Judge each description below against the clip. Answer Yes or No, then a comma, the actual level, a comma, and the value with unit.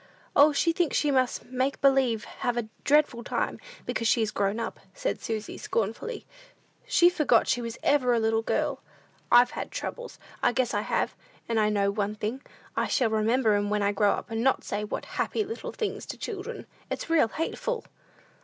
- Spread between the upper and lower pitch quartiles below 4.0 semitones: No, average, 5.1 semitones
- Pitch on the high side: Yes, high, 245 Hz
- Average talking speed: Yes, average, 190 wpm